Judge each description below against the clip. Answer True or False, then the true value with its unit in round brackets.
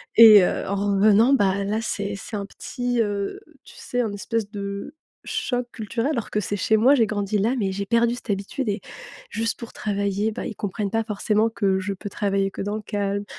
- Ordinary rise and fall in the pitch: False (2.3 semitones)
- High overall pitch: True (210 Hz)